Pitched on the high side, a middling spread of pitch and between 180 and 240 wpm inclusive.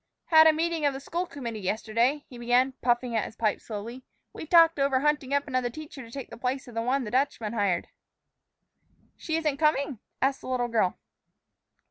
Yes: very high, 260 Hz; average, 3.9 semitones; average, 195 wpm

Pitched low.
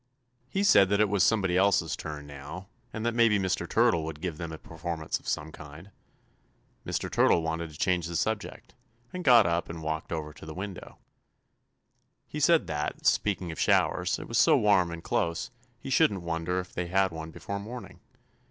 Yes: very low, 90 Hz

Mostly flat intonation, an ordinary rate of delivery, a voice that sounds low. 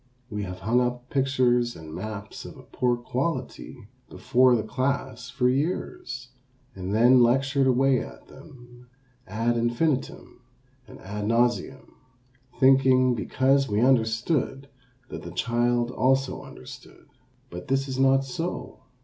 No: narrow, 2.3 semitones; slow, 130 wpm; low, 125 Hz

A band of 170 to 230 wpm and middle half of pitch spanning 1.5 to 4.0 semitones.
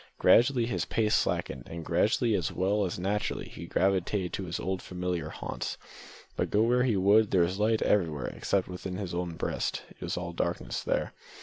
Yes: average, 190 wpm; average, 3.0 semitones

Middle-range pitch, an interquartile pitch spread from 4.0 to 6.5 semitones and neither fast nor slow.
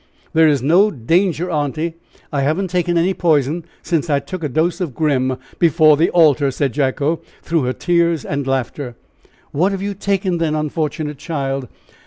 No: medium, 155 Hz; average, 3.4 semitones; average, 170 wpm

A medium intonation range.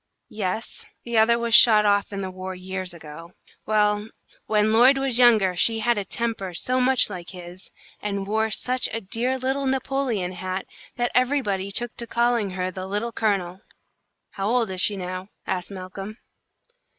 Yes: average, 4.0 semitones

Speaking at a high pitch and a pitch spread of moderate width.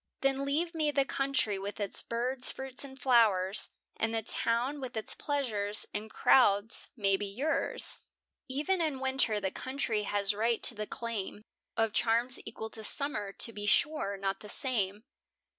Yes: high, 230 Hz; average, 4.5 semitones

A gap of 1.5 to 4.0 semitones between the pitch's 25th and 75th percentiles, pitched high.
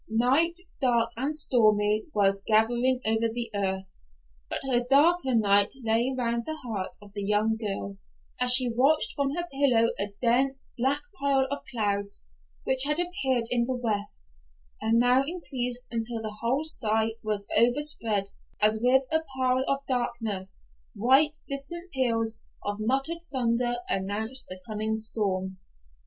Yes: average, 3.7 semitones; high, 235 Hz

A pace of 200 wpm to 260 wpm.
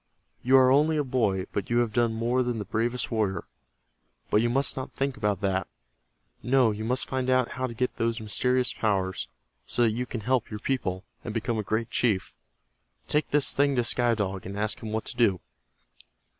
Yes: fast, 205 wpm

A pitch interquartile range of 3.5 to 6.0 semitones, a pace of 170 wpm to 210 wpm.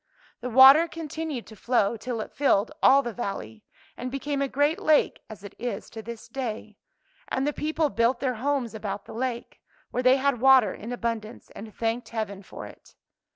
Yes: average, 3.8 semitones; average, 190 wpm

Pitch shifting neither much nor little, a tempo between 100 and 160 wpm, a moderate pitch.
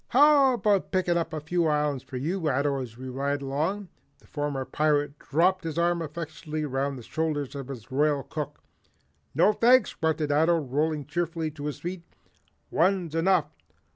No: average, 3.2 semitones; average, 170 wpm; medium, 155 Hz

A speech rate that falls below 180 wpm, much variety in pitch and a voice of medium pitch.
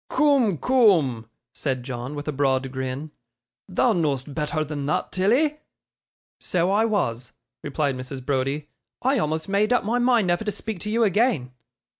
Yes: average, 160 wpm; wide, 8.2 semitones; medium, 155 Hz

